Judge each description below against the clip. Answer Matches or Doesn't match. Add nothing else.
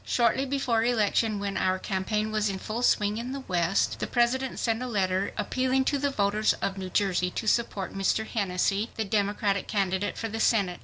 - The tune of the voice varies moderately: Matches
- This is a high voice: Matches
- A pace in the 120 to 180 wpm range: Doesn't match